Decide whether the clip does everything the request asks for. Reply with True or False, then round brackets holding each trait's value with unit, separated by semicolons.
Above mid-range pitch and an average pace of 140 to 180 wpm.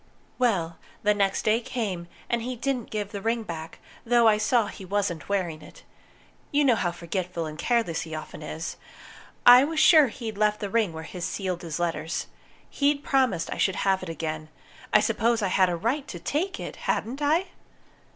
False (205 Hz; 190 wpm)